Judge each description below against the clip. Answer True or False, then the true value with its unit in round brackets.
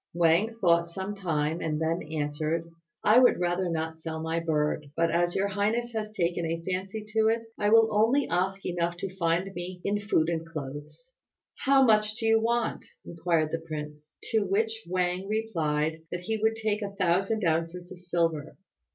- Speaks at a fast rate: False (180 wpm)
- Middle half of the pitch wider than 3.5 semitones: True (4.5 semitones)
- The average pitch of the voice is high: False (180 Hz)